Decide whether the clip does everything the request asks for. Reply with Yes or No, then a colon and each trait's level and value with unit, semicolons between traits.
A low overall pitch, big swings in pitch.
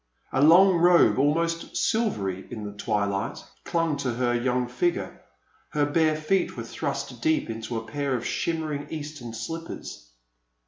No: medium, 145 Hz; wide, 5.8 semitones